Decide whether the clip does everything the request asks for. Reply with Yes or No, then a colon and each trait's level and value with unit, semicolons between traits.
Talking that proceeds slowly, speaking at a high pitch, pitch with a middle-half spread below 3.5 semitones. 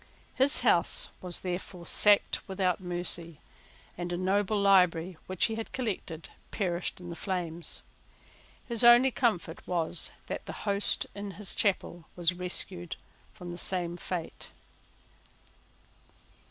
No: slow, 125 wpm; medium, 180 Hz; narrow, 2.6 semitones